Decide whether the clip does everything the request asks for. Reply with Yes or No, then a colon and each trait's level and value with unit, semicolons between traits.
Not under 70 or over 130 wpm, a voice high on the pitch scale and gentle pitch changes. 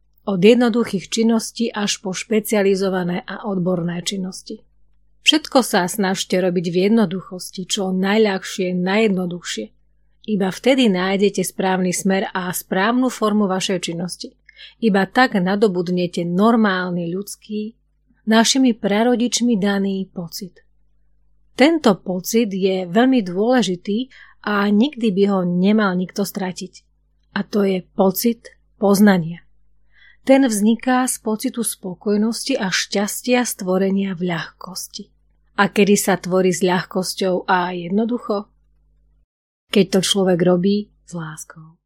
No: slow, 110 wpm; high, 195 Hz; average, 3.3 semitones